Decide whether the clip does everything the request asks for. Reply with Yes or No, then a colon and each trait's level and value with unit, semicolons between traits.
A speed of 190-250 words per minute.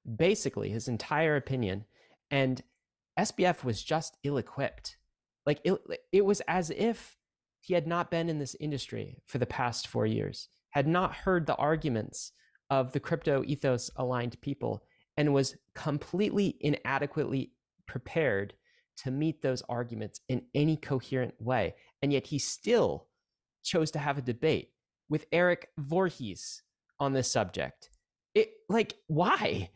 No: average, 140 wpm